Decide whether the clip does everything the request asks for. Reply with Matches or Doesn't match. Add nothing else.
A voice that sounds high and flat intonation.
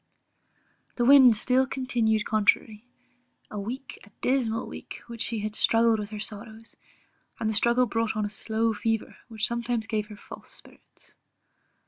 Matches